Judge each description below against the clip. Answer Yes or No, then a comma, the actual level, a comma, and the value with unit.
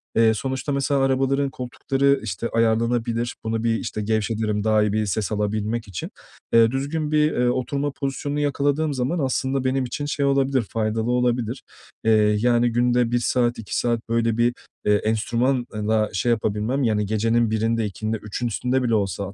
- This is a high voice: No, low, 120 Hz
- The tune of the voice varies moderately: Yes, average, 3.3 semitones